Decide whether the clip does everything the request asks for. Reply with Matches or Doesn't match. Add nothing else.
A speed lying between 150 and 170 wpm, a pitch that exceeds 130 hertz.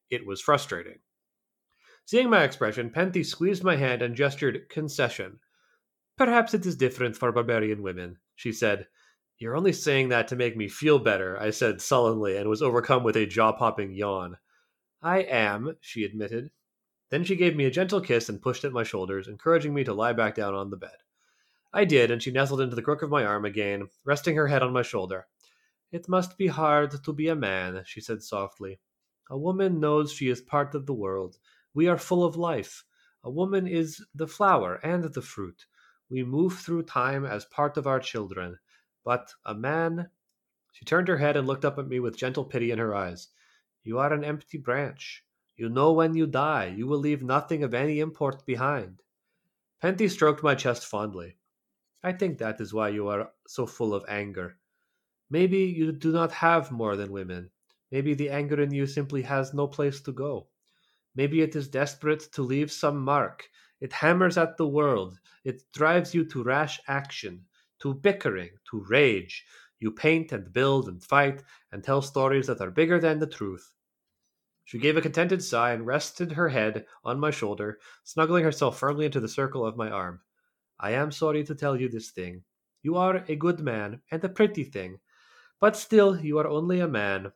Doesn't match